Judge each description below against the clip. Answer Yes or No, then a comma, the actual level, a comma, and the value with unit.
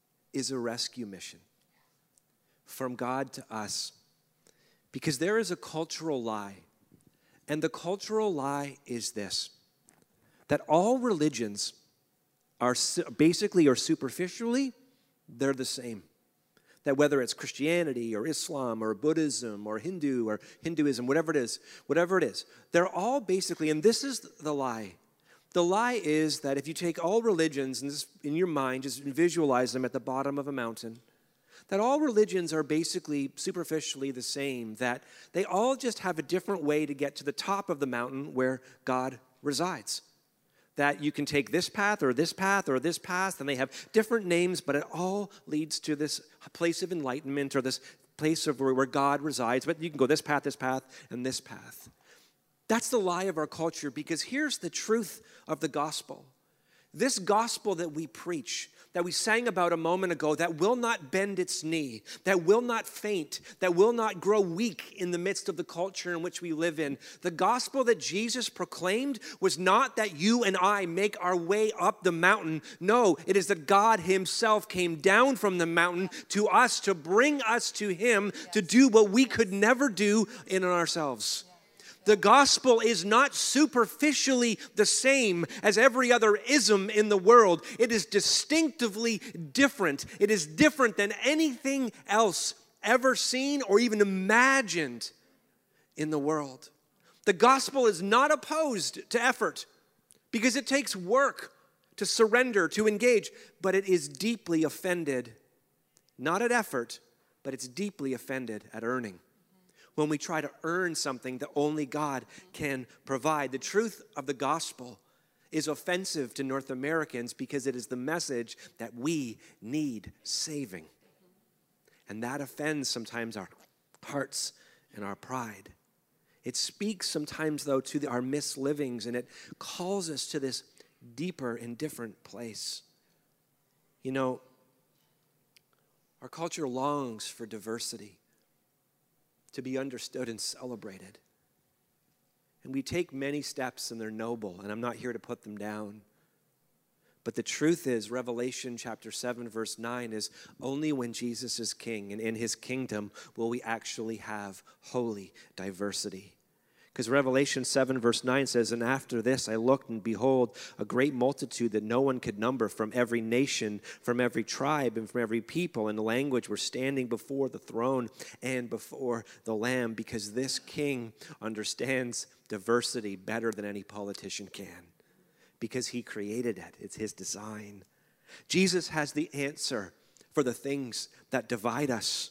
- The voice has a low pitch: No, medium, 150 Hz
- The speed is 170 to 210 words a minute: No, average, 160 wpm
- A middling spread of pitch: No, wide, 7.7 semitones